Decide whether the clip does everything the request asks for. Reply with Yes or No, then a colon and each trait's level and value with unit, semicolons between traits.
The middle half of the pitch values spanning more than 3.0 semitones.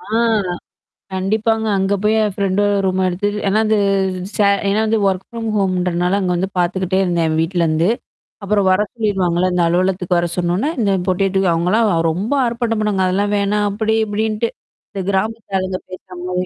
No: average, 2.7 semitones